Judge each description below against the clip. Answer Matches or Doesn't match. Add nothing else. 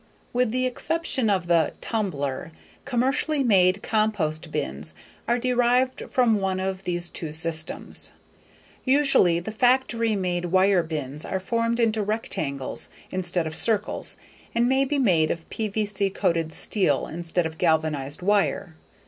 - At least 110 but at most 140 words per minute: Matches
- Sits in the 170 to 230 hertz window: Matches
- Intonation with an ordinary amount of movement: Doesn't match